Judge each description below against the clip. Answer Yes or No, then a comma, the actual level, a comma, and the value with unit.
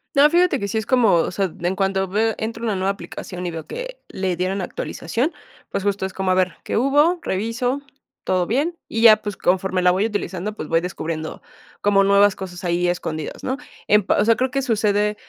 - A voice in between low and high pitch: No, high, 200 Hz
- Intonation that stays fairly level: No, average, 3.8 semitones